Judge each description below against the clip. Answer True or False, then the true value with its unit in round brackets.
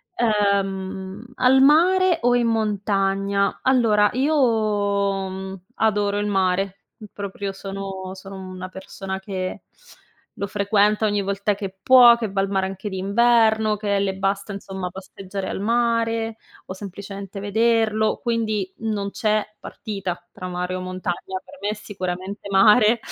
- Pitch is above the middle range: True (200 Hz)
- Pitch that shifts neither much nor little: False (2.3 semitones)